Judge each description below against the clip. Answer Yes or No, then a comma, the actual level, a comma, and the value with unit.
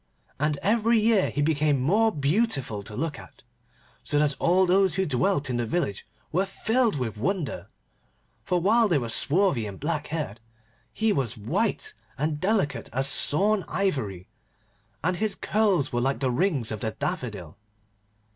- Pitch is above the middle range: No, medium, 150 Hz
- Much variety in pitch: Yes, wide, 7.5 semitones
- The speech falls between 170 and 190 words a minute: No, average, 160 wpm